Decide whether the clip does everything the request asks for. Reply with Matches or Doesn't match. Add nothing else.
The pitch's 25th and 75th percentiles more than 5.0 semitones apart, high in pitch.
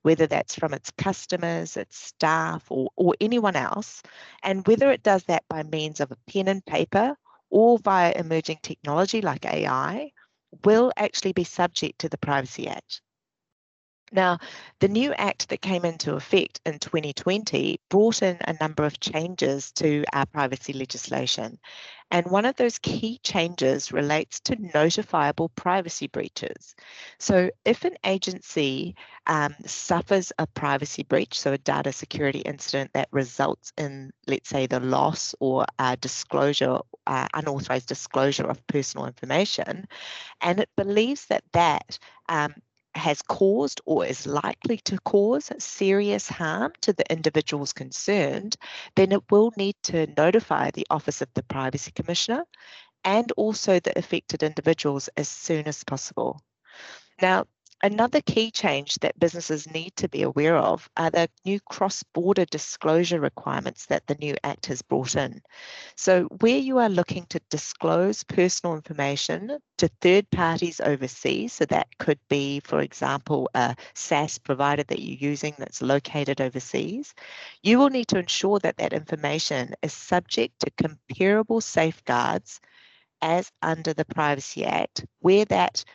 Doesn't match